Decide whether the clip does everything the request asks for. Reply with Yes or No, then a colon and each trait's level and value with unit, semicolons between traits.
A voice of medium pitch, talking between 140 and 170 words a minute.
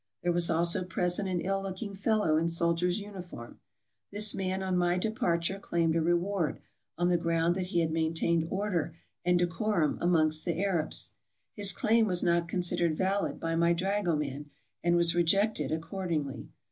Yes: medium, 175 Hz; average, 165 wpm